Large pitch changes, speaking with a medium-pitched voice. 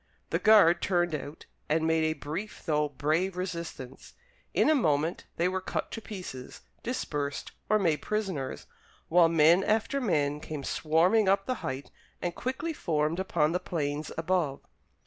No: average, 4.2 semitones; medium, 170 Hz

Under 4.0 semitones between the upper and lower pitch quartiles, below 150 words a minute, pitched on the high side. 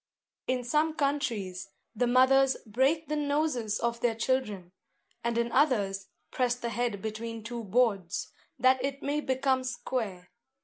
Yes: average, 3.5 semitones; average, 140 wpm; high, 245 Hz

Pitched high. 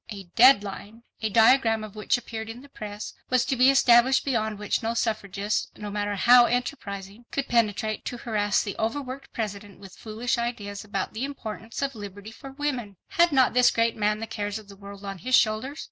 Yes: high, 220 Hz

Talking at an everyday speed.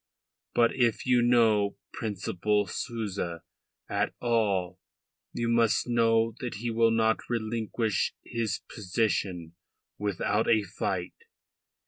No: slow, 105 wpm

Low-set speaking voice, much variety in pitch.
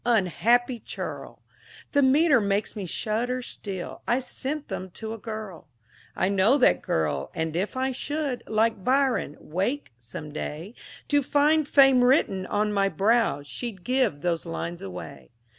No: high, 220 Hz; wide, 5.9 semitones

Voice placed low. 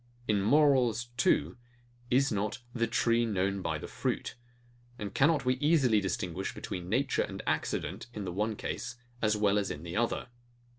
Yes: low, 110 Hz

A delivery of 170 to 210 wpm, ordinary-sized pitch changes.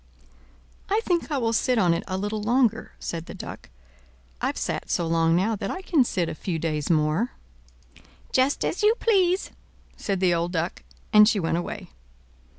No: average, 180 wpm; wide, 7.4 semitones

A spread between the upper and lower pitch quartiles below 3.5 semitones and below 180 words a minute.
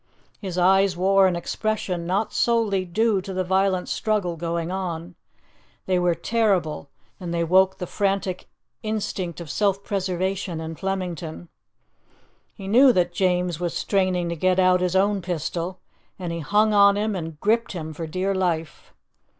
Yes: narrow, 2.4 semitones; average, 160 wpm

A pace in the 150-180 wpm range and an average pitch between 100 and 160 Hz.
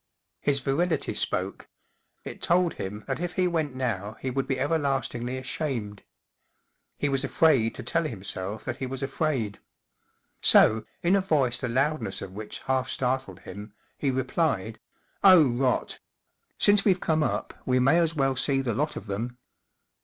Yes: average, 165 wpm; low, 135 Hz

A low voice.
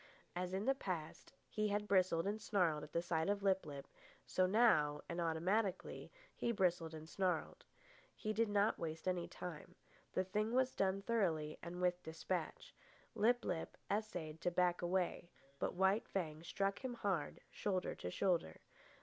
No: medium, 185 Hz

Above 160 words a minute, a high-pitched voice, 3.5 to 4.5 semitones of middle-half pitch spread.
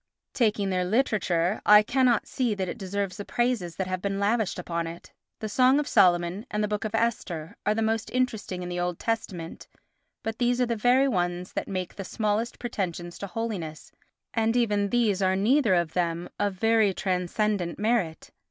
Yes: average, 190 wpm; high, 205 Hz; average, 4.0 semitones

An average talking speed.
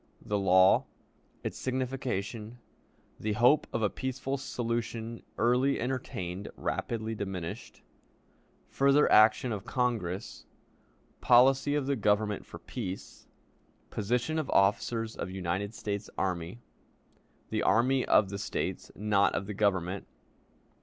No: slow, 115 wpm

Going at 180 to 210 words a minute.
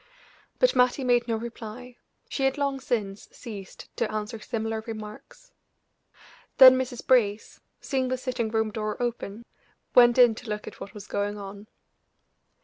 No: average, 150 wpm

